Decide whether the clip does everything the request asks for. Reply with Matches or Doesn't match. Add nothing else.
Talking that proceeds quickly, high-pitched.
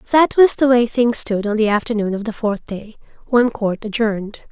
Matches